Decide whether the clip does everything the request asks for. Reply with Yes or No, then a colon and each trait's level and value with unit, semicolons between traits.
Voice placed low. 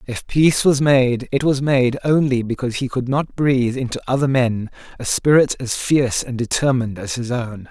Yes: low, 130 Hz